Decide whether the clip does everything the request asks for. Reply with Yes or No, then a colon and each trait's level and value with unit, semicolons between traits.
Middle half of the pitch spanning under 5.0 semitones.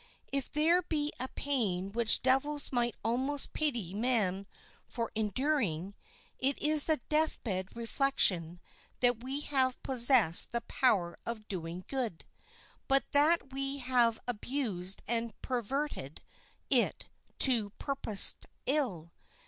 No: average, 5.3 semitones